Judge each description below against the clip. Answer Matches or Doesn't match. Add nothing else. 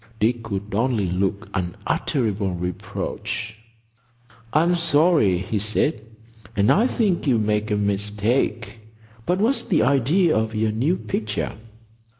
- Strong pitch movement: Matches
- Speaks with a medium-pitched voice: Doesn't match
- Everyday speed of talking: Doesn't match